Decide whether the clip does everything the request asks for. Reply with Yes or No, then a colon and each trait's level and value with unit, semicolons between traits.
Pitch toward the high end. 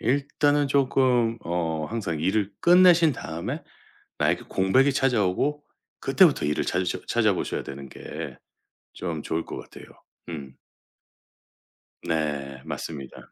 No: low, 100 Hz